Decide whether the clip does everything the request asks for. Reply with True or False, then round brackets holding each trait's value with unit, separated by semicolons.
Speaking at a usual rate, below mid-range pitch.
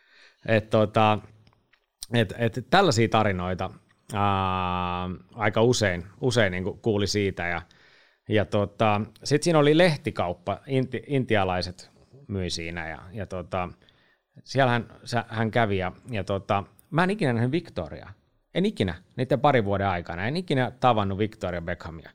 True (135 wpm; 105 Hz)